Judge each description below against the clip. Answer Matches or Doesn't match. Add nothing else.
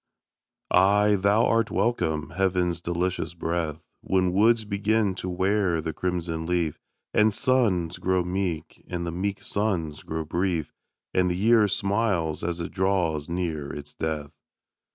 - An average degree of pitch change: Matches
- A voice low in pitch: Matches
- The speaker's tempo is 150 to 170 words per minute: Doesn't match